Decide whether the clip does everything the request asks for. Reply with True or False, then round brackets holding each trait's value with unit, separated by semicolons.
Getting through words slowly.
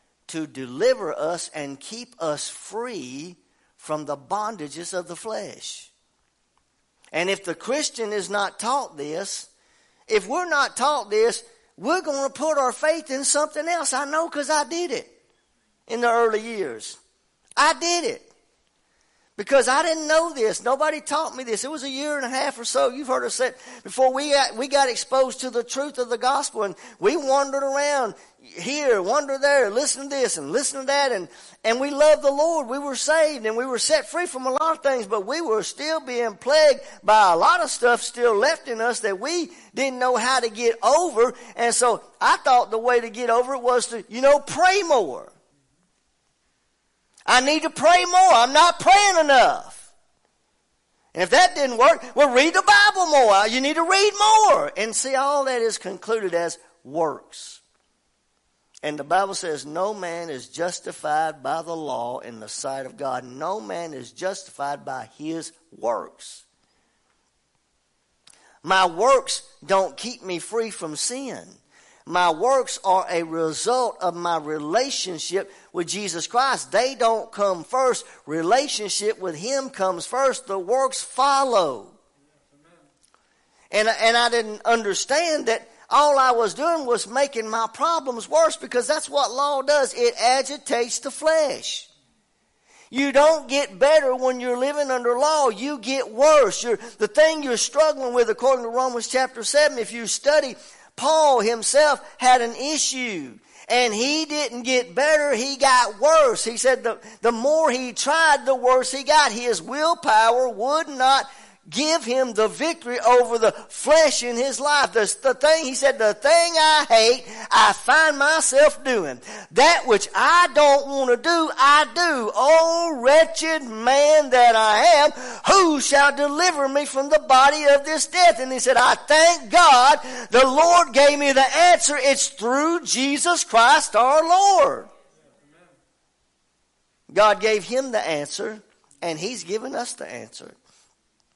False (170 wpm)